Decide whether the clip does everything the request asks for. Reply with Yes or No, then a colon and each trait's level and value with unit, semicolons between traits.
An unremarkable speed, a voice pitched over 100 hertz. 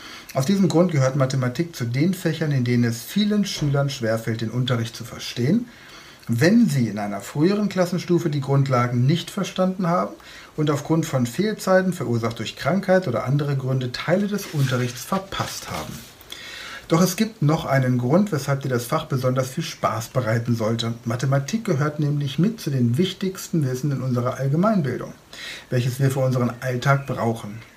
Yes: average, 165 wpm; medium, 140 Hz